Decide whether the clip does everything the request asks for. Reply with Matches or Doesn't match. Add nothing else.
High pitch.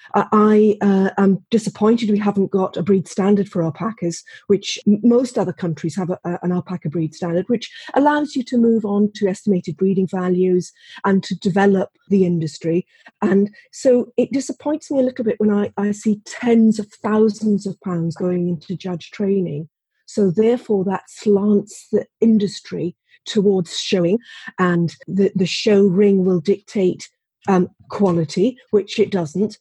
Matches